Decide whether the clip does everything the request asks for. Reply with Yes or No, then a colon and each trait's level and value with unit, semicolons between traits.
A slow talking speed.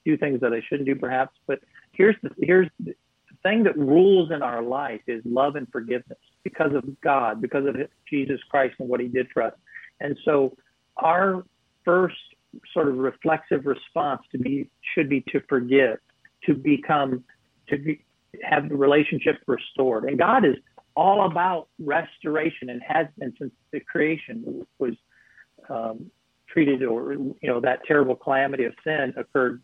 No: average, 165 wpm